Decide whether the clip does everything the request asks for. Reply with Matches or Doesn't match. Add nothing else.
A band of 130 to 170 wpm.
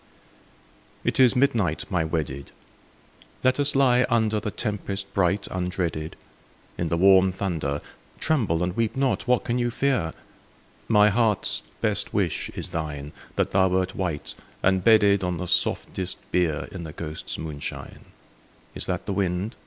Matches